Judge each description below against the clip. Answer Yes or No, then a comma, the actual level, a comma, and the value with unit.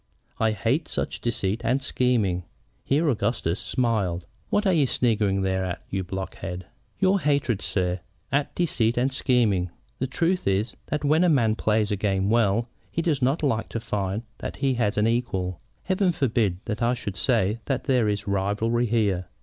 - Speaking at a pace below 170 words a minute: No, average, 175 wpm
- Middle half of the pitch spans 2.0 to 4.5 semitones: No, average, 5.1 semitones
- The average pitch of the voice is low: Yes, low, 115 Hz